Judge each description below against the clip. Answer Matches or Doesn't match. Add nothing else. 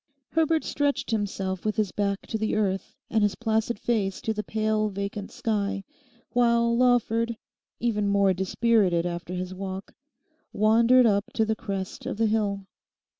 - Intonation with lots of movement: Doesn't match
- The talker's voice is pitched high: Matches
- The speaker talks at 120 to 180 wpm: Matches